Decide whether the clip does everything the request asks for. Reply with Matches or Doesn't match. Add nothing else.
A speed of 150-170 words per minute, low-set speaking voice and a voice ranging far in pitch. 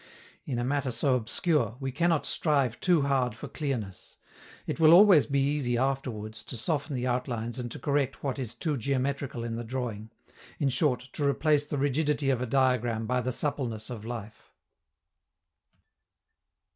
Doesn't match